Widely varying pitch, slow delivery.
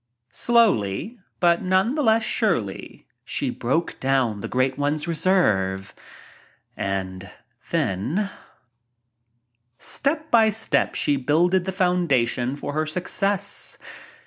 Yes: wide, 8.4 semitones; slow, 105 wpm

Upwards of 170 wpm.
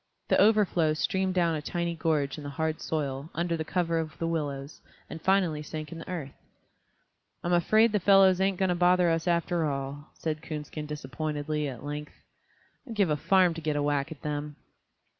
Yes: average, 190 wpm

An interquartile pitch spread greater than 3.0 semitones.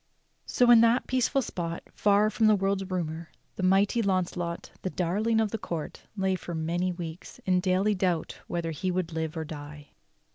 Yes: average, 3.4 semitones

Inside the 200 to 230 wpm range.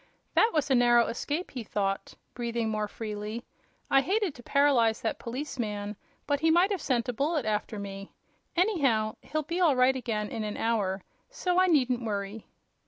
No: average, 175 wpm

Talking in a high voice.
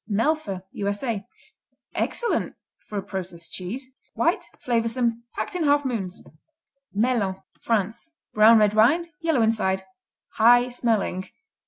Yes: high, 225 Hz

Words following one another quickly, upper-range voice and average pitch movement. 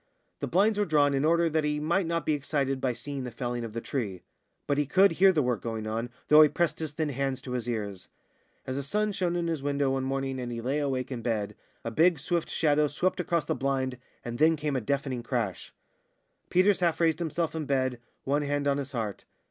No: fast, 235 wpm; medium, 140 Hz; average, 4.2 semitones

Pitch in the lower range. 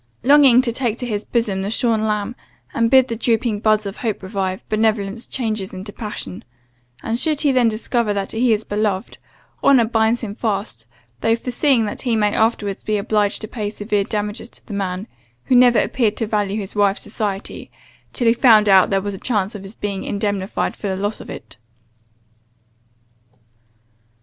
No: high, 215 Hz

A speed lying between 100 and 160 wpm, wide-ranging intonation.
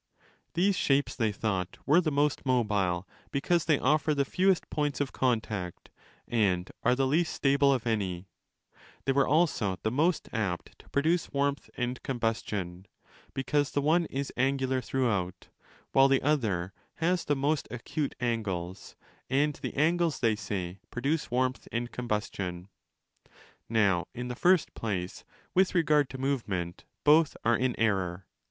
Yes: average, 150 wpm; wide, 5.9 semitones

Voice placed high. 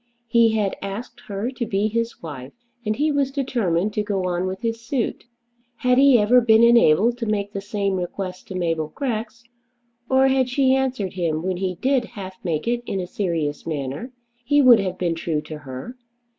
Yes: high, 210 Hz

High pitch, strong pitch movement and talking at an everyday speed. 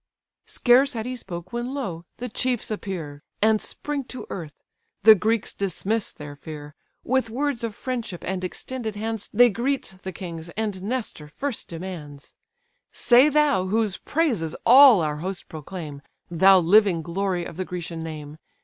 Yes: high, 195 Hz; wide, 6.0 semitones; average, 155 wpm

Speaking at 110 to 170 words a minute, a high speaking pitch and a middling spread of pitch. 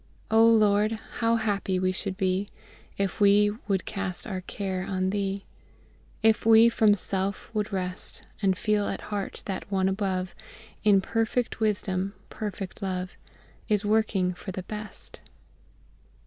No: average, 140 wpm; high, 200 Hz; narrow, 2.1 semitones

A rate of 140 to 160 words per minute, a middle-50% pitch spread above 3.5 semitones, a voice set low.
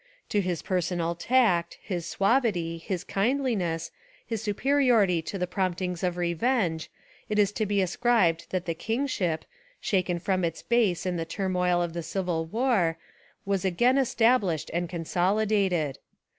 No: average, 145 wpm; average, 4.1 semitones; medium, 185 Hz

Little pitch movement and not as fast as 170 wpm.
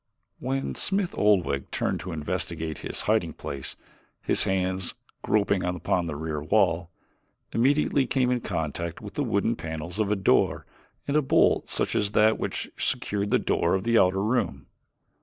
No: average, 5.1 semitones; average, 160 wpm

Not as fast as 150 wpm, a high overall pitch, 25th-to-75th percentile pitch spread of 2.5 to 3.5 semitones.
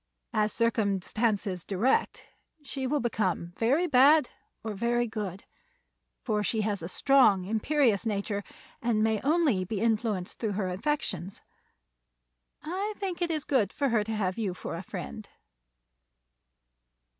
No: slow, 135 wpm; high, 220 Hz; average, 4.9 semitones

